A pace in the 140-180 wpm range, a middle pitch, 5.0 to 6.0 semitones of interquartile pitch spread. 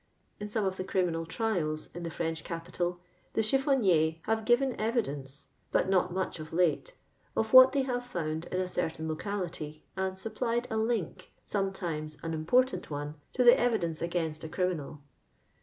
Yes: average, 175 wpm; medium, 180 Hz; wide, 5.6 semitones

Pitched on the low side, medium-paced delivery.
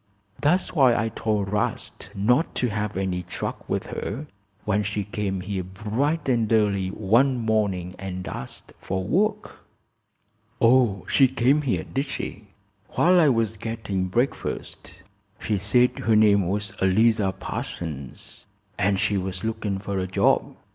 Yes: low, 105 Hz; average, 145 wpm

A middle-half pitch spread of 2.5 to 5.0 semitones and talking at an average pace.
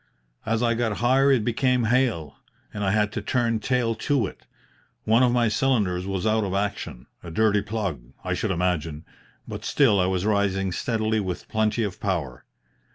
Yes: average, 3.7 semitones; average, 180 wpm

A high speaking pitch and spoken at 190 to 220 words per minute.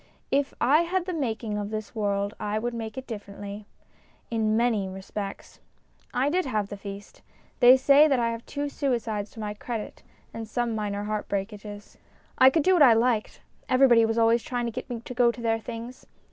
Yes: high, 230 Hz; average, 200 wpm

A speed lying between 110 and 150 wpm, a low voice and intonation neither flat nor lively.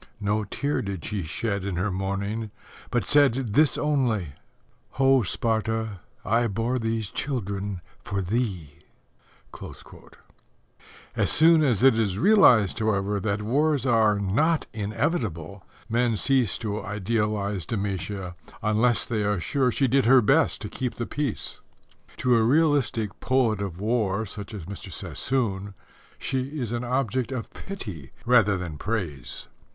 Yes: slow, 135 wpm; low, 110 Hz; average, 4.2 semitones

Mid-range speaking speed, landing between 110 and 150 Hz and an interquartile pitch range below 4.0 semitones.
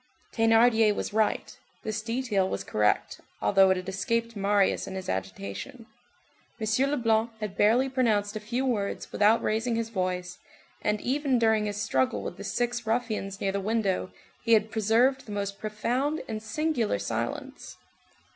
No: average, 155 wpm; high, 220 Hz; average, 2.8 semitones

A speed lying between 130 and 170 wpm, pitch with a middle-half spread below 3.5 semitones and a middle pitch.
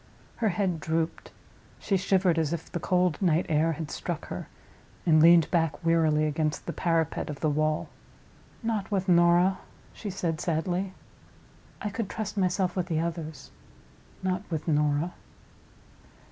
Yes: average, 145 wpm; average, 2.8 semitones; medium, 170 Hz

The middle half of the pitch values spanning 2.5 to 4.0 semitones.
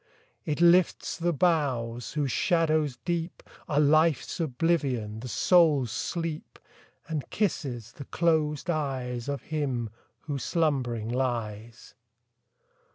No: average, 5.0 semitones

